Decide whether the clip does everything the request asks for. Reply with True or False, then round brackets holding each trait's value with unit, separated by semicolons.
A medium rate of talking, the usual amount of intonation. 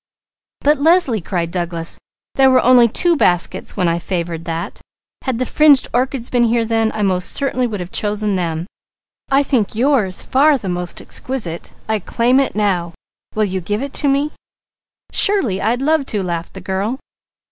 False (175 wpm; 6.5 semitones)